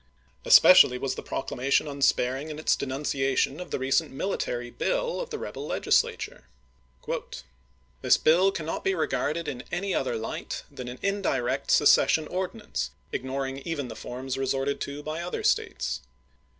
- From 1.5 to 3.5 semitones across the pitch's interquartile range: No, average, 3.9 semitones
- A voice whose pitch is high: No, medium, 140 Hz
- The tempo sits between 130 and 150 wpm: Yes, average, 145 wpm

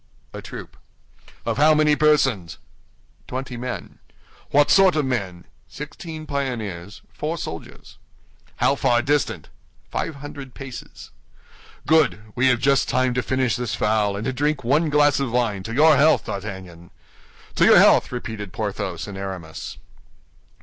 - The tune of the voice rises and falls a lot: Yes, wide, 5.9 semitones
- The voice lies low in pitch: Yes, low, 125 Hz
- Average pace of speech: Yes, average, 145 wpm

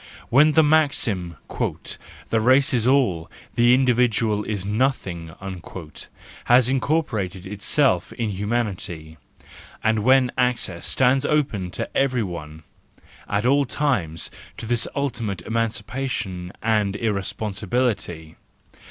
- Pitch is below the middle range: Yes, low, 110 Hz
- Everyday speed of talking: No, slow, 110 wpm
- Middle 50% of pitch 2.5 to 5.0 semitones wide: No, wide, 5.4 semitones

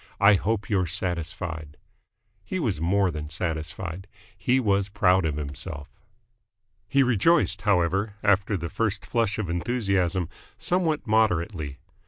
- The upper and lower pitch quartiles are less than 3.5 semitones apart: No, average, 4.3 semitones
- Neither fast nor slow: No, slow, 125 wpm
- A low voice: Yes, very low, 95 Hz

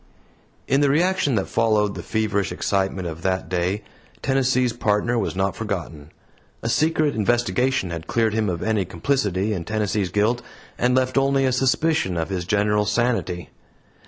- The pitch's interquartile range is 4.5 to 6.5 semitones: Yes, average, 4.9 semitones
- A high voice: No, low, 105 Hz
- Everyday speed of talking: Yes, average, 160 wpm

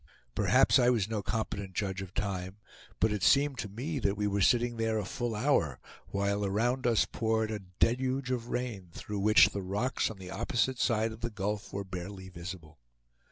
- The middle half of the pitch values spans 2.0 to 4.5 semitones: Yes, average, 3.5 semitones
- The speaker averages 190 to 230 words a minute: Yes, average, 195 wpm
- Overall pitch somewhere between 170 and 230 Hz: No, low, 105 Hz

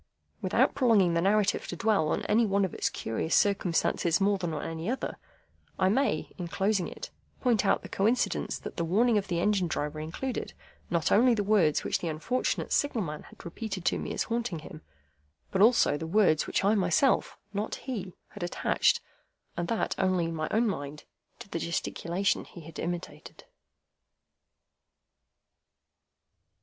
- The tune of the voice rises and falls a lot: No, average, 4.3 semitones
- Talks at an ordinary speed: Yes, average, 165 wpm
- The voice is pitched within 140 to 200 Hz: Yes, high, 190 Hz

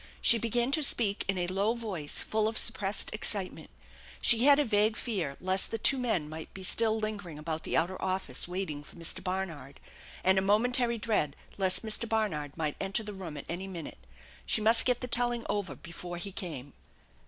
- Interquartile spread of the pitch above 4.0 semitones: Yes, average, 4.6 semitones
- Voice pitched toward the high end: Yes, high, 195 Hz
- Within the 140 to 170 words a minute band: No, average, 195 wpm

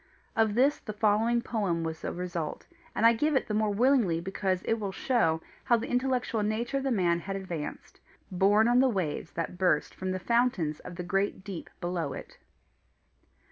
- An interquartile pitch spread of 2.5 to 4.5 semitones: No, average, 4.9 semitones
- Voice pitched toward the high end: Yes, high, 200 Hz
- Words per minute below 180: No, average, 190 wpm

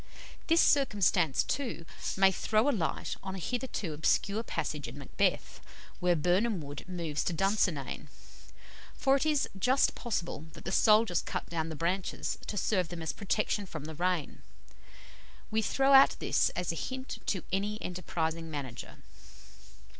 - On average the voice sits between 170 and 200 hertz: Yes, medium, 185 Hz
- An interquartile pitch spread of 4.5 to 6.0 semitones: Yes, average, 5.2 semitones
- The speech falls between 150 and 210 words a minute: Yes, average, 155 wpm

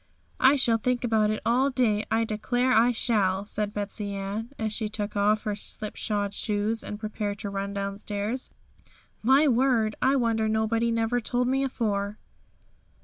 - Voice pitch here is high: Yes, high, 220 Hz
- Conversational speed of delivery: Yes, average, 160 wpm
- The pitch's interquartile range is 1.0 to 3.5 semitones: Yes, average, 2.7 semitones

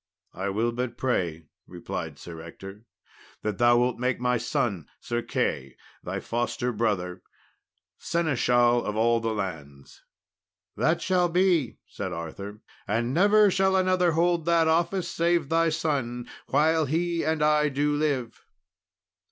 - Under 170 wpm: Yes, average, 140 wpm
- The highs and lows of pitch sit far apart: Yes, wide, 7.6 semitones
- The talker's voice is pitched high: No, low, 125 Hz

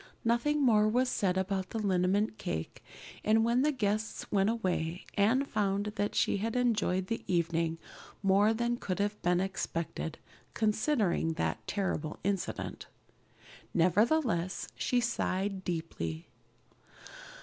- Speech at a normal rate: No, slow, 125 wpm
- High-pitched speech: Yes, high, 200 Hz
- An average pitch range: Yes, average, 3.8 semitones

